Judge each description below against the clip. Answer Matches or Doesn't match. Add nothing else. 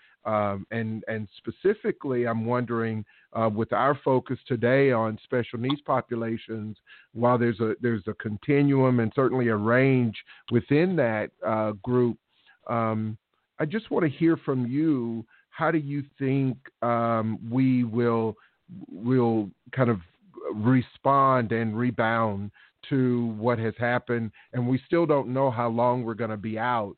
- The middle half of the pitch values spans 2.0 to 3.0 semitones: Matches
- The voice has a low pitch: Matches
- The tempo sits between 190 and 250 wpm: Doesn't match